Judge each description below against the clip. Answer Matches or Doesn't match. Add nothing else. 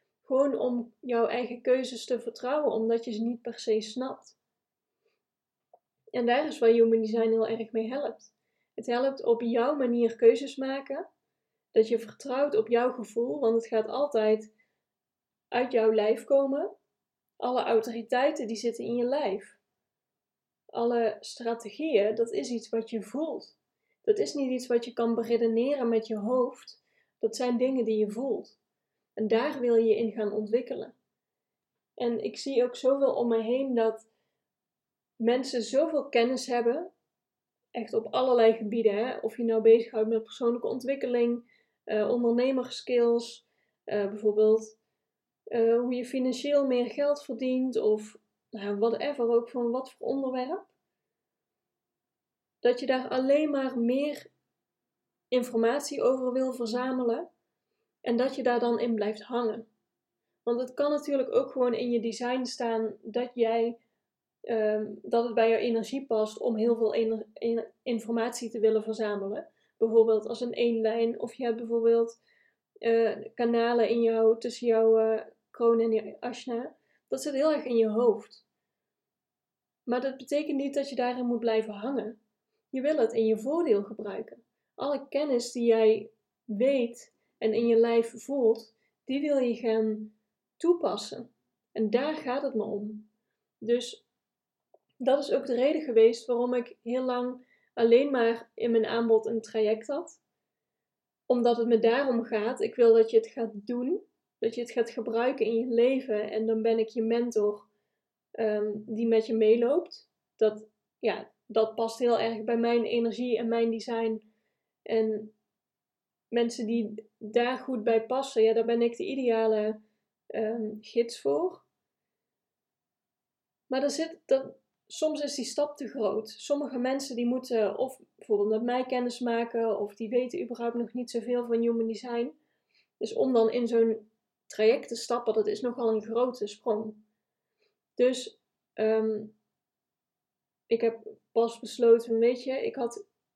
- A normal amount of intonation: Doesn't match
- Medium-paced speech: Matches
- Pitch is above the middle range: Matches